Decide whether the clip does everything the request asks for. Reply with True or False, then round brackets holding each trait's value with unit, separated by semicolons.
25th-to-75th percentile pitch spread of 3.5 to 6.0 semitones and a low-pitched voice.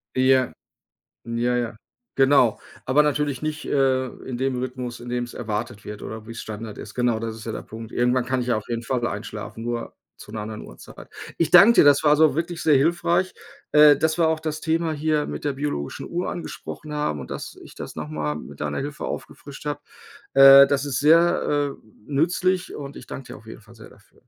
True (4.3 semitones; 130 Hz)